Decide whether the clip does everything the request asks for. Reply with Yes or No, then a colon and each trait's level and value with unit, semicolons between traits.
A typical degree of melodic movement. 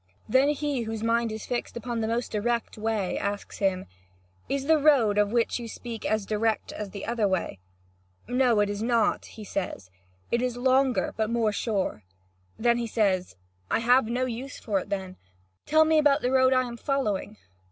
Yes: average, 3.2 semitones